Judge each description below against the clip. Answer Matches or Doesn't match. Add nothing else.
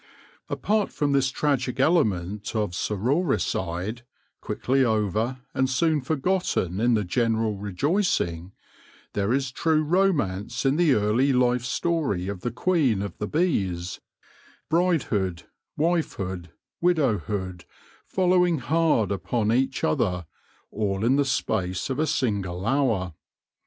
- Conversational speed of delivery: Doesn't match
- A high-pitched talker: Doesn't match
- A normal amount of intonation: Doesn't match